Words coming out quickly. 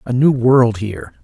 No: average, 195 wpm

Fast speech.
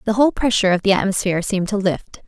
Yes: fast, 235 wpm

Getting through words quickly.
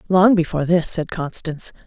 No: average, 160 wpm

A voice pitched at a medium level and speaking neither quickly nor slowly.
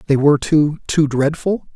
Yes: medium, 150 Hz; average, 170 wpm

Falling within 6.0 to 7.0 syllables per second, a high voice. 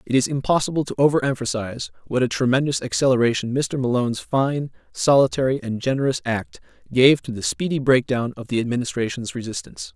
No: 6.1 syllables/s; low, 130 Hz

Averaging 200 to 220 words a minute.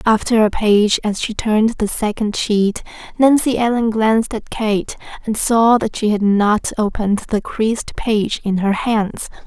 No: average, 170 wpm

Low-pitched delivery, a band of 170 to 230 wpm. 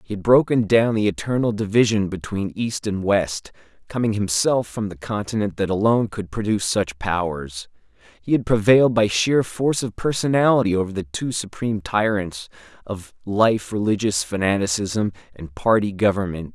No: low, 105 Hz; average, 150 wpm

